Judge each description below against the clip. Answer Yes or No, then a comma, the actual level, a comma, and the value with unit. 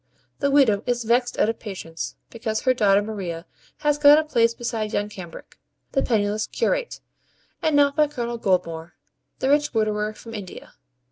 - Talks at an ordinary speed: Yes, average, 165 wpm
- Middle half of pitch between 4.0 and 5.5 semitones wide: Yes, average, 4.8 semitones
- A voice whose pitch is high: Yes, high, 225 Hz